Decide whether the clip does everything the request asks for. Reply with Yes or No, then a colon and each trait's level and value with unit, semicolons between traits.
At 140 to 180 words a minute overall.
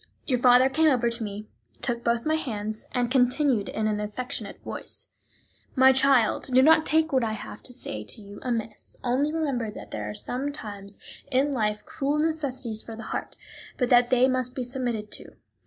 No: average, 190 wpm